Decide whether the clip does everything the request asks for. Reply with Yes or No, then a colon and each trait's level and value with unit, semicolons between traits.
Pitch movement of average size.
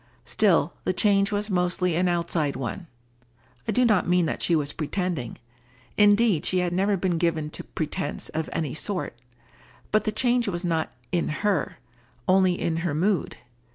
Yes: average, 3.6 semitones